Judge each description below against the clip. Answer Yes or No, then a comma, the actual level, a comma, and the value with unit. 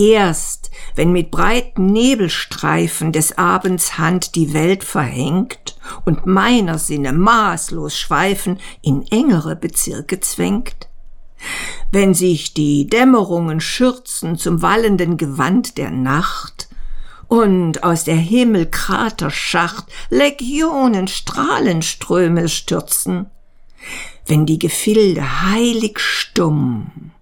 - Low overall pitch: No, medium, 180 Hz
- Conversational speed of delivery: No, slow, 95 wpm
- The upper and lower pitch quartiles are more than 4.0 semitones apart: Yes, average, 5.1 semitones